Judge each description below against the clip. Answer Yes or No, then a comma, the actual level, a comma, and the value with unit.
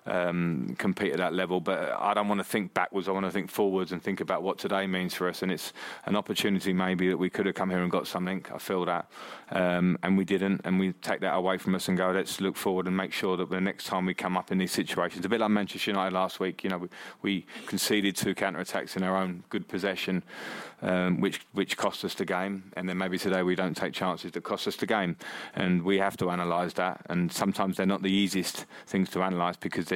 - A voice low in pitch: Yes, very low, 95 Hz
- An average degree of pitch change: No, narrow, 1.0 semitones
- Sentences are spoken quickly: Yes, fast, 260 wpm